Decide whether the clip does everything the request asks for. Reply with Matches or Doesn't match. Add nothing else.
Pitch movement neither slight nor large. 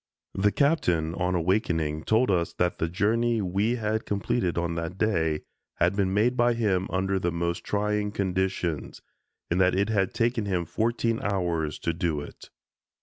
Matches